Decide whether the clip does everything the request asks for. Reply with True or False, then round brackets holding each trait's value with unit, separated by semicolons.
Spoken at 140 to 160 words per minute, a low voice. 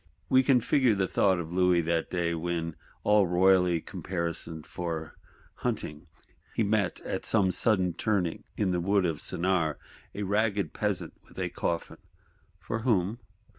True (150 wpm; 90 Hz)